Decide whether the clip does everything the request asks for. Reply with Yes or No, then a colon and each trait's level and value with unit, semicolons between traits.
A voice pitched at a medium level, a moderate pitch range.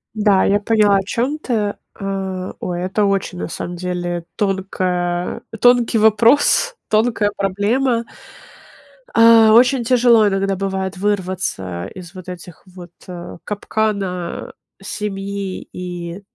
No: high, 195 Hz; average, 3.1 semitones